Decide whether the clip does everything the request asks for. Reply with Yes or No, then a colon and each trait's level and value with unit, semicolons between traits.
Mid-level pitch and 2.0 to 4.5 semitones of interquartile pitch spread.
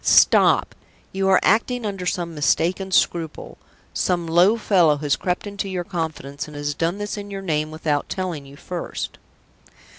Yes: medium, 175 Hz; average, 3.9 semitones